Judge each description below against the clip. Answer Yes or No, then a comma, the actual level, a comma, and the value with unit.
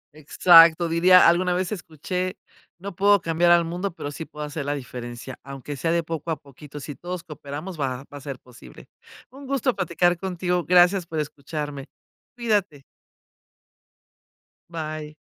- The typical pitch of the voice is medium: Yes, medium, 165 Hz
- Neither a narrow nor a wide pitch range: Yes, average, 3.6 semitones